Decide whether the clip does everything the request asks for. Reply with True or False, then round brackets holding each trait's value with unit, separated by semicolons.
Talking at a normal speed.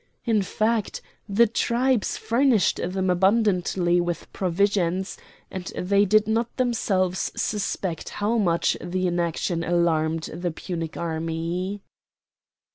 False (110 wpm)